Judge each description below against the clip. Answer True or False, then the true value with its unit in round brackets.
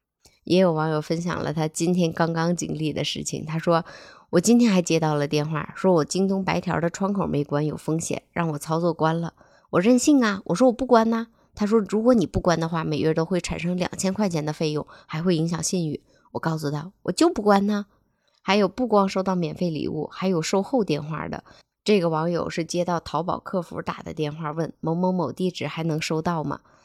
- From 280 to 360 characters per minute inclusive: True (315 characters per minute)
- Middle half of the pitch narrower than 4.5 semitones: True (3.4 semitones)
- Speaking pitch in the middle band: True (170 Hz)